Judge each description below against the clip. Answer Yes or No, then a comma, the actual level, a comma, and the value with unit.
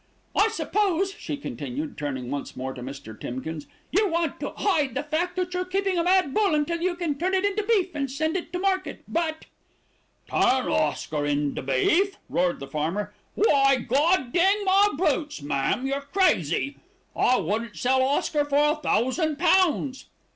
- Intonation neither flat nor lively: No, wide, 8.5 semitones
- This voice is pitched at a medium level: No, very high, 295 Hz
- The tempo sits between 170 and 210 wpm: Yes, average, 175 wpm